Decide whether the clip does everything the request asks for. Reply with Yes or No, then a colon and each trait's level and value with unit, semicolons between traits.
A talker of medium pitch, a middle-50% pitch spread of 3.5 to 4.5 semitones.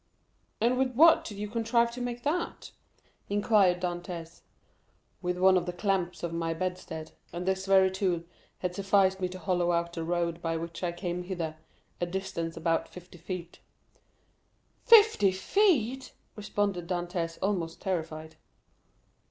No: medium, 180 Hz; average, 3.0 semitones